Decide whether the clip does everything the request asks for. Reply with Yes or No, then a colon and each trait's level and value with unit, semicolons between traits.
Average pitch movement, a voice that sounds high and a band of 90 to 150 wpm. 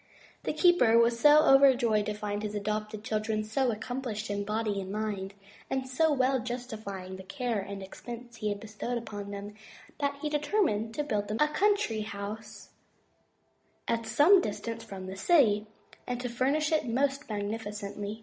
No: average, 4.0 semitones; high, 220 Hz; average, 165 wpm